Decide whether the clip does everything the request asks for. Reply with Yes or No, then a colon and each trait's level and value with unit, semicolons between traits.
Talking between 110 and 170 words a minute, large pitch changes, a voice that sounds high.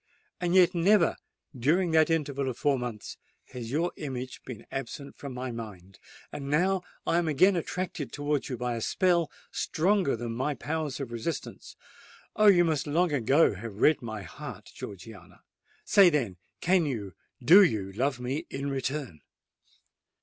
No: average, 150 wpm; wide, 5.9 semitones; medium, 140 Hz